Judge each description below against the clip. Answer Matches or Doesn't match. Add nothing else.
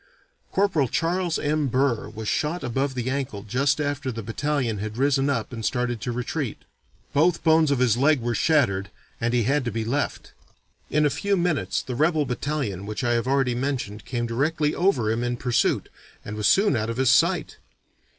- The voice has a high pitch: Doesn't match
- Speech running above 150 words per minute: Matches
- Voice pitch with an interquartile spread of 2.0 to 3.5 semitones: Doesn't match